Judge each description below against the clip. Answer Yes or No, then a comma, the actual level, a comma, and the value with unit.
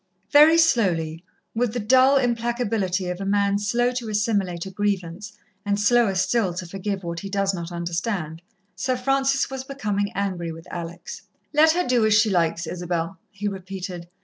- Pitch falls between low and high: No, high, 200 Hz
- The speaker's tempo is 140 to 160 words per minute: No, average, 170 wpm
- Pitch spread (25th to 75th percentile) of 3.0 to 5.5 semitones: Yes, average, 5.1 semitones